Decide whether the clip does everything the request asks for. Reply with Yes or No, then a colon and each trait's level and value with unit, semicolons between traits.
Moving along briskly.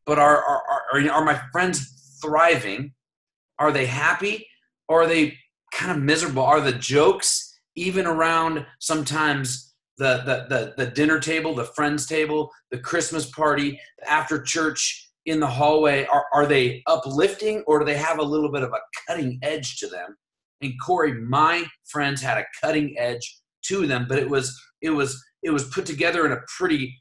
No: average, 175 wpm